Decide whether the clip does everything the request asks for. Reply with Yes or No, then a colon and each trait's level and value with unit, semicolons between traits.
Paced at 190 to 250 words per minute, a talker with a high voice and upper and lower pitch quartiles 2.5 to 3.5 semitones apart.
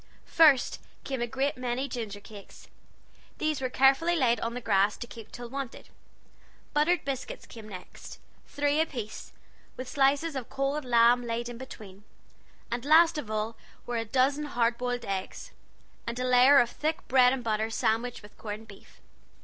No: average, 165 wpm; high, 245 Hz; average, 3.2 semitones